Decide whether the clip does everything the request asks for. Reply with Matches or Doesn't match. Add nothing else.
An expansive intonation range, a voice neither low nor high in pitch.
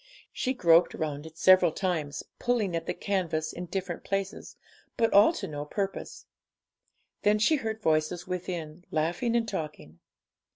Doesn't match